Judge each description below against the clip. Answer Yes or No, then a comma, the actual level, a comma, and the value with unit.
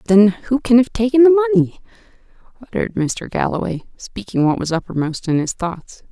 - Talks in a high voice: Yes, high, 195 Hz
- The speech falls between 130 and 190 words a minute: Yes, average, 165 wpm